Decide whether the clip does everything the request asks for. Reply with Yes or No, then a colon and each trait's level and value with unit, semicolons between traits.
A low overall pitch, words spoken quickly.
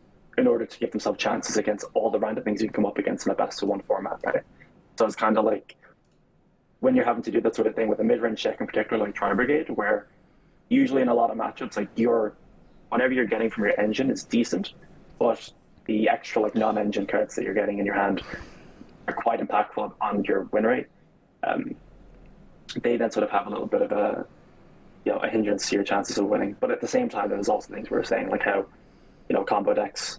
No: high, 245 Hz; fast, 240 wpm